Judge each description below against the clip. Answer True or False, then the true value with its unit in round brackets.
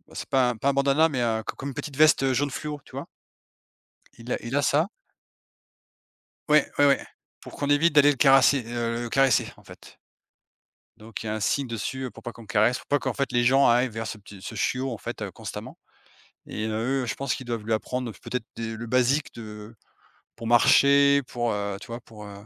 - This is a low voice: True (125 Hz)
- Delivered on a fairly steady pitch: False (3.5 semitones)